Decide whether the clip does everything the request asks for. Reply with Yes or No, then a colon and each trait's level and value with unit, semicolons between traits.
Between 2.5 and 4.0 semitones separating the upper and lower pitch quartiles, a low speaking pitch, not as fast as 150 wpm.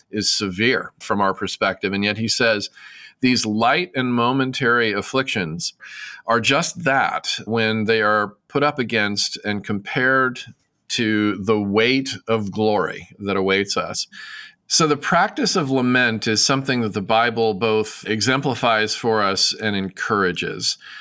Yes: average, 3.4 semitones; low, 110 Hz; average, 140 wpm